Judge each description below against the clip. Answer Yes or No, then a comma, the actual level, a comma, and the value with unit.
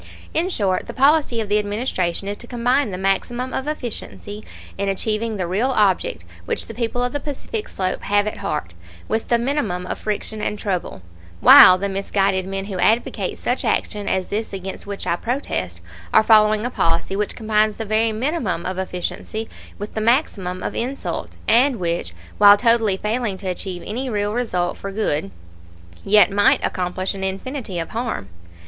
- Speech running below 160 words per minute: No, average, 180 wpm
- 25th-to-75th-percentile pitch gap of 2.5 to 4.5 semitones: Yes, average, 3.7 semitones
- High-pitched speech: Yes, high, 210 Hz